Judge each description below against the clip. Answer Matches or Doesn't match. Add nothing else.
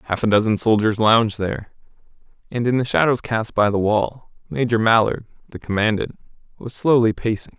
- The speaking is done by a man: Matches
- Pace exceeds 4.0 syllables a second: Matches